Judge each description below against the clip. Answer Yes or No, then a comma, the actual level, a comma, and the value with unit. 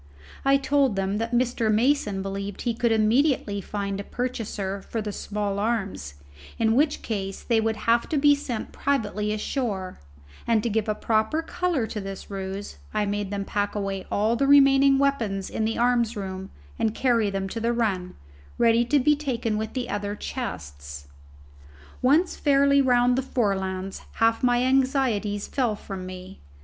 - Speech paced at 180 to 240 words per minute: No, average, 170 wpm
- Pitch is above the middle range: Yes, high, 220 Hz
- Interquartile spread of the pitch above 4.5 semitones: No, average, 4.1 semitones